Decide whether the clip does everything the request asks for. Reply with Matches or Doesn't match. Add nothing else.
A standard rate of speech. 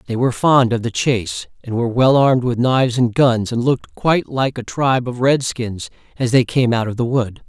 Doesn't match